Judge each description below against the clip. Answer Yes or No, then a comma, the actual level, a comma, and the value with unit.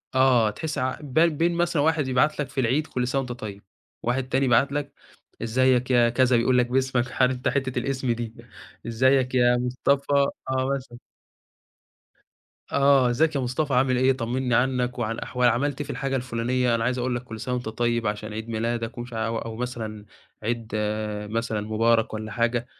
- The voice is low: Yes, low, 125 Hz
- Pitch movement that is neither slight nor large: No, narrow, 2.2 semitones